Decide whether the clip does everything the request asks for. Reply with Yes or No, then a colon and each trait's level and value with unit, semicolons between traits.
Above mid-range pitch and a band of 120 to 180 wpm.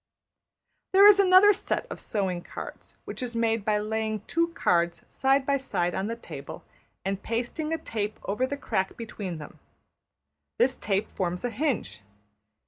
Yes: high, 220 Hz; average, 160 wpm